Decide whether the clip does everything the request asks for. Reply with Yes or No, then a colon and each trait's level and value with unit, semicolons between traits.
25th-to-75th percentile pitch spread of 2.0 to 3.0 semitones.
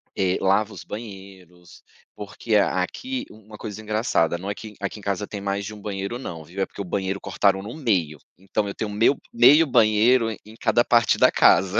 Yes: narrow, 2.4 semitones